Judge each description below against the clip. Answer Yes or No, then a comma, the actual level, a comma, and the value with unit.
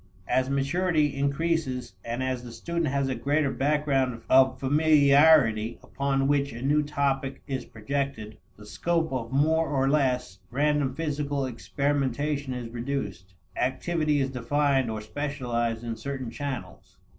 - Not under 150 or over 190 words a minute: No, slow, 135 wpm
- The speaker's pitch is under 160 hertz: Yes, low, 135 Hz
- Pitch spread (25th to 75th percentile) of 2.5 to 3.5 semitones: Yes, average, 2.8 semitones